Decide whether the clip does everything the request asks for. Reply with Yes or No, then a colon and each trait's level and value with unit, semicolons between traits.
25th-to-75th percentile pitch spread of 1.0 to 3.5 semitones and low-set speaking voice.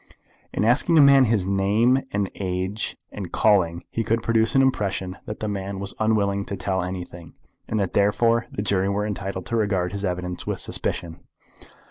Yes: average, 2.7 semitones; low, 100 Hz